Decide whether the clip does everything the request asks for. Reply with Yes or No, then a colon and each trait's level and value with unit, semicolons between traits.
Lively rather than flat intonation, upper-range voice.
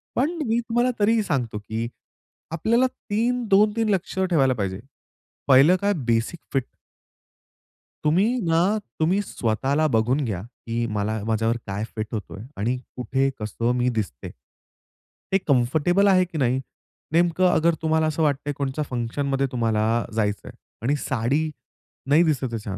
No: wide, 7.7 semitones; medium, 140 Hz